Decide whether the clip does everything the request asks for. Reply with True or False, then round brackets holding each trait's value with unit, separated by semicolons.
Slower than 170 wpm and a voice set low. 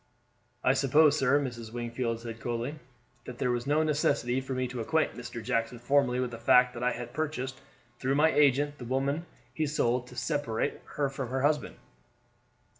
False (185 wpm; 130 Hz)